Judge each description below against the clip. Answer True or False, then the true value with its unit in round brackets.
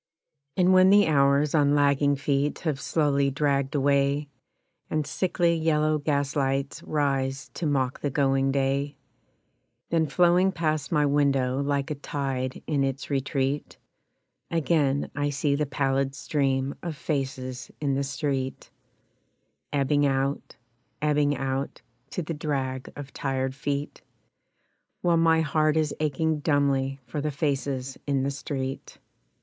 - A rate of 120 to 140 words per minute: True (135 wpm)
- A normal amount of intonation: False (1.9 semitones)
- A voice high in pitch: False (140 Hz)